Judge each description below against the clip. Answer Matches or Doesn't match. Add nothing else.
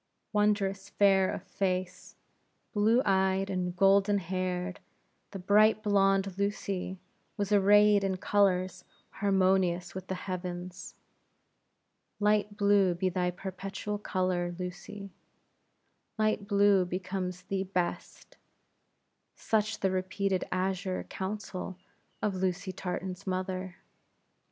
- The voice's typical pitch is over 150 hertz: Matches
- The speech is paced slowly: Matches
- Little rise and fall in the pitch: Matches